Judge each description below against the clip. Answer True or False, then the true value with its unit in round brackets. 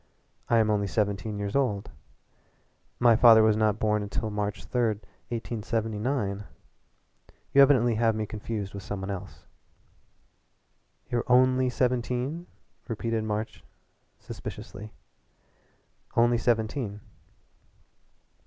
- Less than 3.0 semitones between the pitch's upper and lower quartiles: True (2.6 semitones)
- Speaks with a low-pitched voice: True (110 Hz)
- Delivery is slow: True (105 wpm)